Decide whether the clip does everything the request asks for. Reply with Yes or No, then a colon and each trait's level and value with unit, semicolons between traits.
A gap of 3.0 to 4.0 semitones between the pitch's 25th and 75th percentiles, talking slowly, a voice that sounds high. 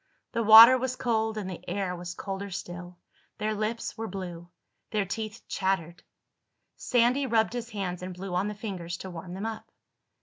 No: average, 3.7 semitones; average, 175 wpm; high, 200 Hz